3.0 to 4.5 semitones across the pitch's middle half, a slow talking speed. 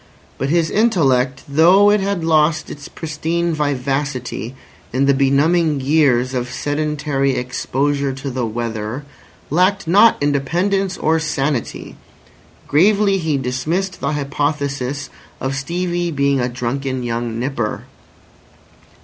Yes: average, 3.8 semitones; slow, 115 wpm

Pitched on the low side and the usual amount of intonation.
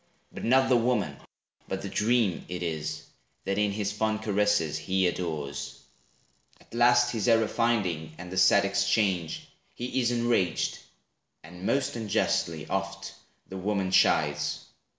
Yes: low, 100 Hz; average, 4.4 semitones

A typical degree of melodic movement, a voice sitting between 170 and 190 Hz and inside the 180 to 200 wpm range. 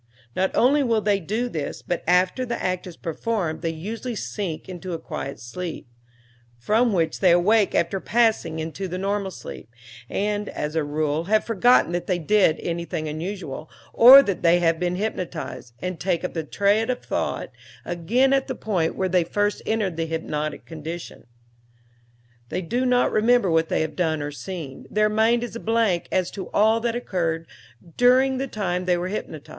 Yes: average, 5.0 semitones; medium, 185 Hz; average, 185 wpm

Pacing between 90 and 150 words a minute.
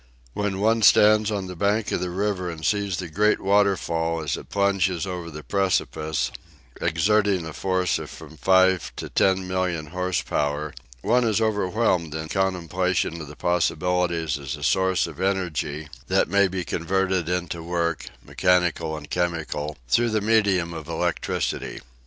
No: average, 160 wpm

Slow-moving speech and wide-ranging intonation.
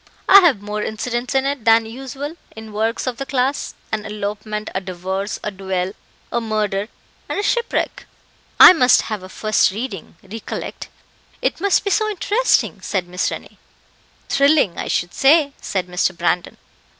No: average, 160 wpm; wide, 5.7 semitones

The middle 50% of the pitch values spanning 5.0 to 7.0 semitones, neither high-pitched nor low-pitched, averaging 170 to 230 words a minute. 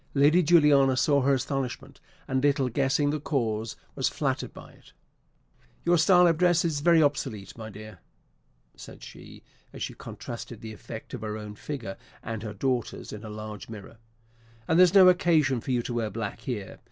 No: wide, 5.6 semitones; low, 130 Hz; average, 180 wpm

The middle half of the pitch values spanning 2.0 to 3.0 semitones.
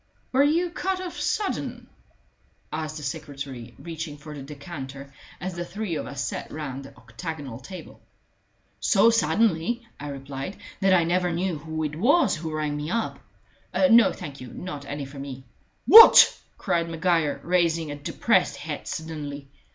No: average, 4.3 semitones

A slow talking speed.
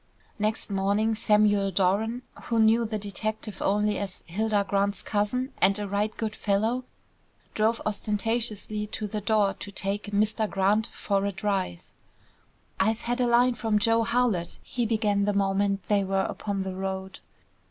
No: average, 155 wpm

